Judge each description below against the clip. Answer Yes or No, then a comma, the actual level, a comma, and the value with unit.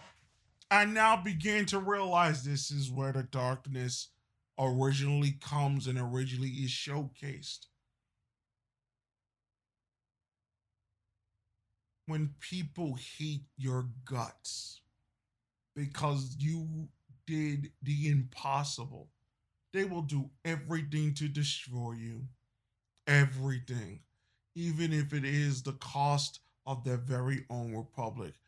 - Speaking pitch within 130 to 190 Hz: Yes, low, 135 Hz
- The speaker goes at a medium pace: No, slow, 95 wpm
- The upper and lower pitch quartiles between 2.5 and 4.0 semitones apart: Yes, average, 3.7 semitones